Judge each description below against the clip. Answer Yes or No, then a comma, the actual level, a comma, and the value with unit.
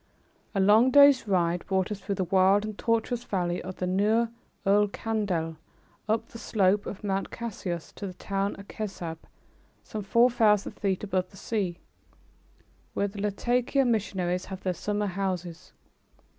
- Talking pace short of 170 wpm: Yes, average, 155 wpm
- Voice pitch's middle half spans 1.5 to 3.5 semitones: Yes, average, 2.8 semitones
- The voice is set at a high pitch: Yes, high, 200 Hz